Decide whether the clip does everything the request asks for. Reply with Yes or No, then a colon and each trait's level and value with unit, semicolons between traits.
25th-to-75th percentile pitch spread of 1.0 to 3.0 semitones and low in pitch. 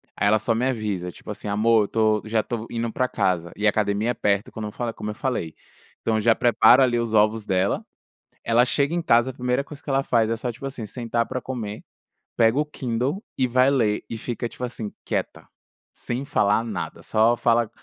Yes: average, 2.7 semitones; low, 115 Hz